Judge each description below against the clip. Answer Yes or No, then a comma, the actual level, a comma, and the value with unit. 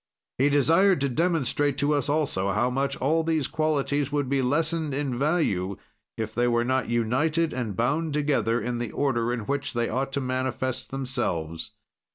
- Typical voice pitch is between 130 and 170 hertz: Yes, low, 135 Hz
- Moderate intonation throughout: Yes, average, 3.6 semitones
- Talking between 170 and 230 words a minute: Yes, average, 175 wpm